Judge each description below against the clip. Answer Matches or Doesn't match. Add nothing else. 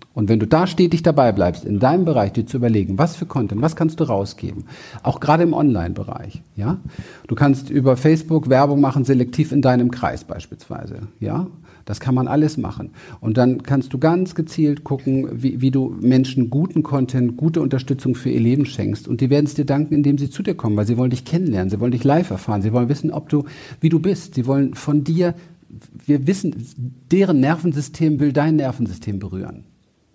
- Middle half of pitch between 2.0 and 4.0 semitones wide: Doesn't match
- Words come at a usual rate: Doesn't match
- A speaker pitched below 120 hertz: Doesn't match